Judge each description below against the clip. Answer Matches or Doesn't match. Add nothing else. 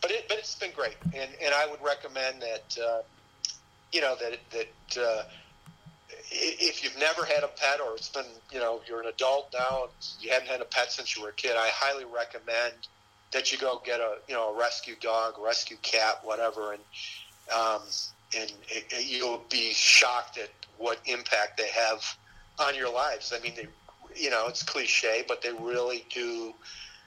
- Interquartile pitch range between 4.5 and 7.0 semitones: Doesn't match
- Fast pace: Doesn't match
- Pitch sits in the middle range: Doesn't match